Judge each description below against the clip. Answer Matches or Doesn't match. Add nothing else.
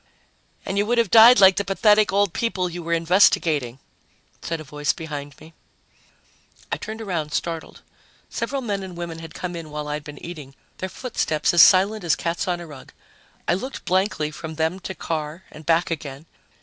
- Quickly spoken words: Doesn't match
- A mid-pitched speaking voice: Matches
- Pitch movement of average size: Matches